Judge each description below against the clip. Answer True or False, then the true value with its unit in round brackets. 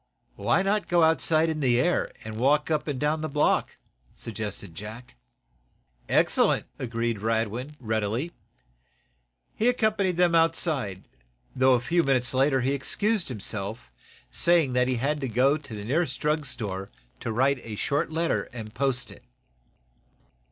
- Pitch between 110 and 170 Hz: True (135 Hz)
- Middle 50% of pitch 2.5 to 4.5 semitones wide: False (5.6 semitones)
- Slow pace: False (145 wpm)